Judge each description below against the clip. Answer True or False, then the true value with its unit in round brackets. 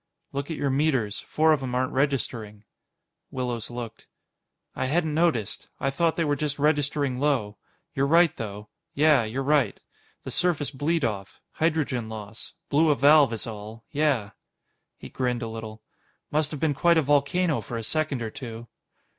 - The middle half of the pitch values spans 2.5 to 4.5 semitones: False (4.9 semitones)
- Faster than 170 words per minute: False (165 wpm)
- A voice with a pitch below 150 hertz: True (135 Hz)